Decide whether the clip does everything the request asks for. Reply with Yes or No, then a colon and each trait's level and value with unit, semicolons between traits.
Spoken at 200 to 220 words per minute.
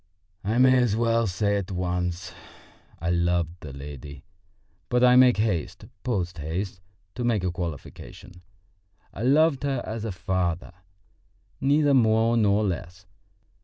No: slow, 135 wpm